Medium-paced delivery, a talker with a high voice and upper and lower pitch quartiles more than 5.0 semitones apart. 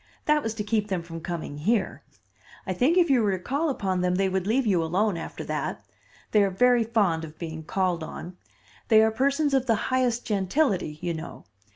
No: fast, 210 wpm; high, 200 Hz; wide, 5.5 semitones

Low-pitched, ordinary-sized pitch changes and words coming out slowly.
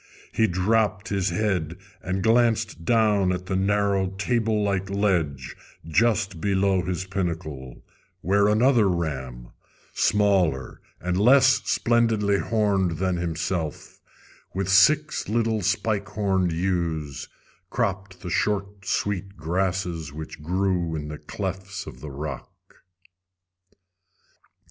Yes: very low, 95 Hz; average, 3.2 semitones; slow, 110 wpm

